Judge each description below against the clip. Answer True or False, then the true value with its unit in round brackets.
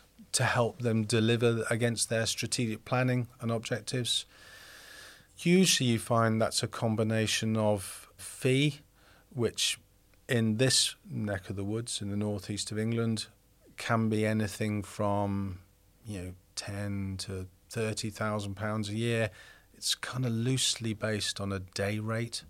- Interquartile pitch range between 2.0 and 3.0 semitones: True (2.4 semitones)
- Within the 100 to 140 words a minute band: True (135 wpm)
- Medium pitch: False (110 Hz)